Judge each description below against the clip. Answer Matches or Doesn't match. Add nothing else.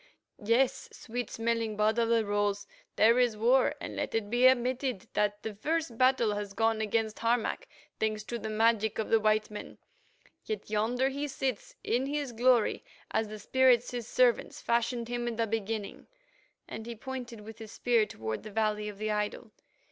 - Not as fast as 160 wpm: Doesn't match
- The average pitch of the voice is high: Matches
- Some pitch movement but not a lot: Doesn't match